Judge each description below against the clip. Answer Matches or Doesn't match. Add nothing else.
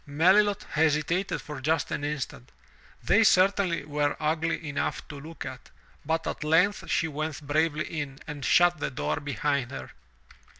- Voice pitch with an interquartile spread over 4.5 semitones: Doesn't match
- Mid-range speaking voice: Matches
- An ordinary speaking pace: Matches